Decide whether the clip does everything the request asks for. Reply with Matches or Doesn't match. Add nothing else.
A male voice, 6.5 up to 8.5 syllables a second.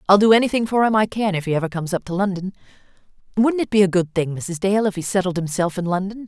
Doesn't match